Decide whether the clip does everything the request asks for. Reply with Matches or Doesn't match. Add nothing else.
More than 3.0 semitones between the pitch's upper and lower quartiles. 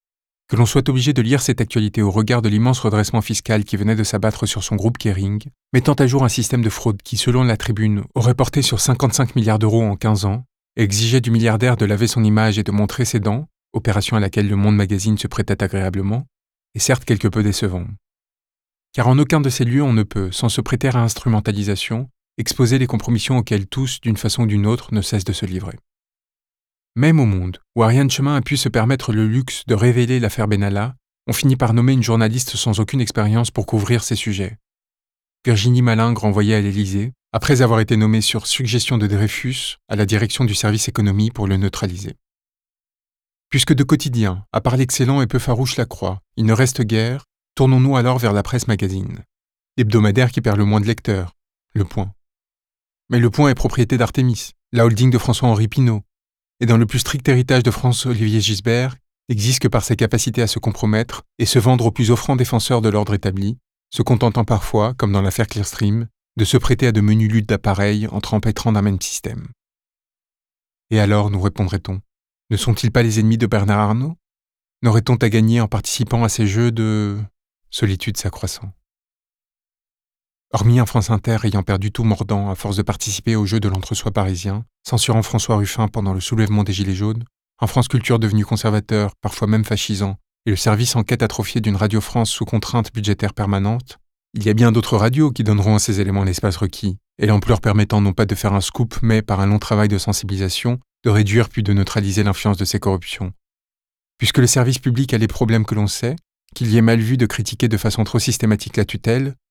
Doesn't match